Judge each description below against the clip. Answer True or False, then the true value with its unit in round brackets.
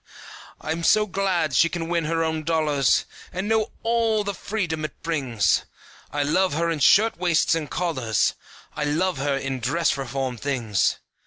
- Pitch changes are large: False (4.7 semitones)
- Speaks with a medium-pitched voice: True (160 Hz)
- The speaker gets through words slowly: False (165 wpm)